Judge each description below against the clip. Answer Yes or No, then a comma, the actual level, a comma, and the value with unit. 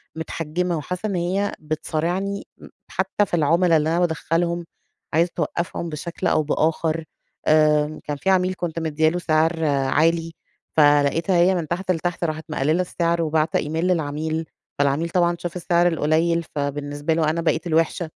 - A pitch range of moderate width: No, narrow, 2.0 semitones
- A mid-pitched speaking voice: Yes, medium, 165 Hz